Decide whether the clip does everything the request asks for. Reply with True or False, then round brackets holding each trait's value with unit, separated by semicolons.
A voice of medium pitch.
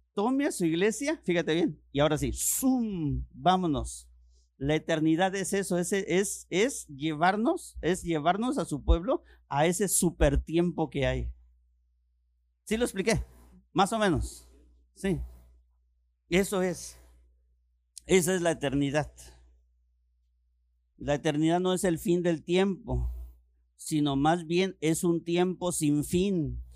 True (155 Hz)